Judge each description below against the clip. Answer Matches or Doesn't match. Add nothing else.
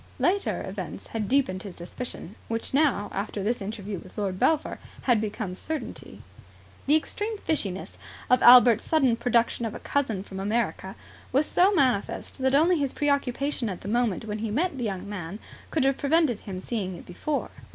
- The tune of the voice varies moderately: Doesn't match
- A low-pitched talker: Doesn't match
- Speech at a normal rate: Matches